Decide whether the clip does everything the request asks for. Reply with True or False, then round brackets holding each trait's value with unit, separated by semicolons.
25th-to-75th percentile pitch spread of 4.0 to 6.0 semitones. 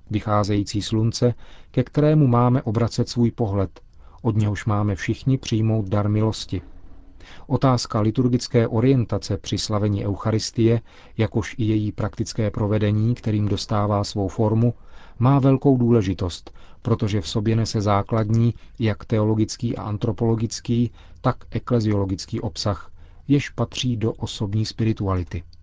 False (2.5 semitones)